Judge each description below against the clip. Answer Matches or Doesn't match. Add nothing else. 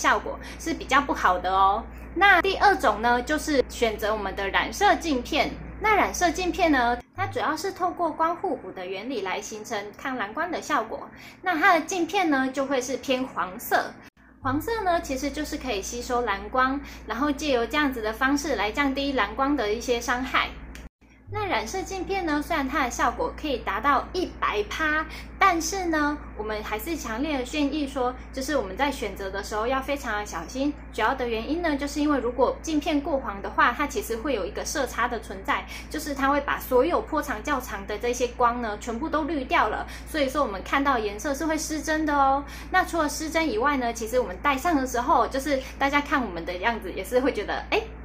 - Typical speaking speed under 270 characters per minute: Doesn't match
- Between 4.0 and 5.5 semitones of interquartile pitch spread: Matches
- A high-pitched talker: Matches